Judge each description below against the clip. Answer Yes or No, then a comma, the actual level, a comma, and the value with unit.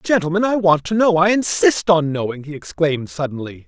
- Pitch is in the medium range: Yes, medium, 170 Hz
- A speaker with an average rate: Yes, average, 195 wpm